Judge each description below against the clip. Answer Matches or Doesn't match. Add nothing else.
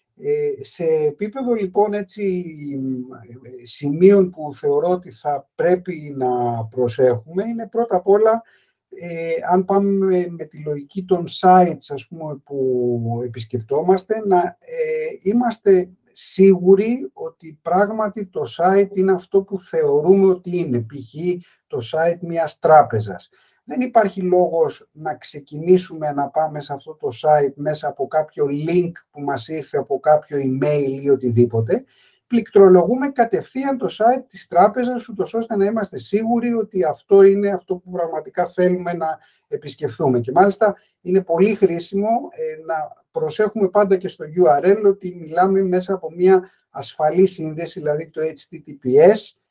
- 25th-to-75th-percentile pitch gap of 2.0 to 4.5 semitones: Doesn't match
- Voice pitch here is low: Doesn't match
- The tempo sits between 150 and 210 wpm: Doesn't match